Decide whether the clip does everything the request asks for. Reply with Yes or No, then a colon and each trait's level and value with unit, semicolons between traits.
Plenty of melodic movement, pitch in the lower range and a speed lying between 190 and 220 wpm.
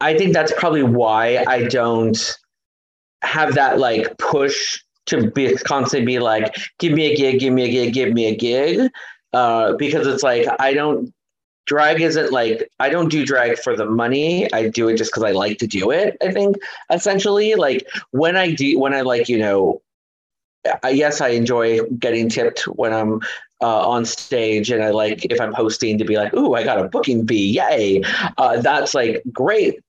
Yes: wide, 5.7 semitones; low, 120 Hz; average, 195 wpm